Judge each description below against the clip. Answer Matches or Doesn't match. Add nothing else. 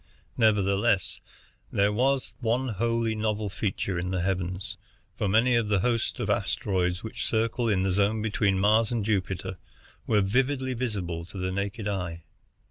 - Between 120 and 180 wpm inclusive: Matches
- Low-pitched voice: Matches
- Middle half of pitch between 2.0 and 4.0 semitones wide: Matches